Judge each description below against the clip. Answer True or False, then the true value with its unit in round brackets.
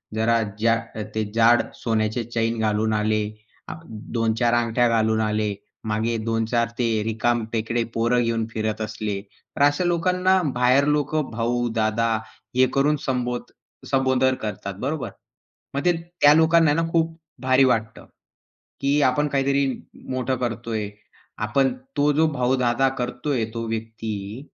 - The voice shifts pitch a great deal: False (3.3 semitones)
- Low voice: True (120 Hz)